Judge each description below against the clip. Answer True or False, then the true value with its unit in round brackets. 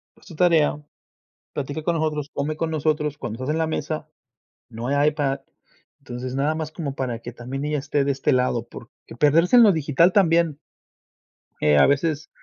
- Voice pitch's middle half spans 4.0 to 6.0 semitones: False (2.9 semitones)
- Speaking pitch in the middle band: True (150 Hz)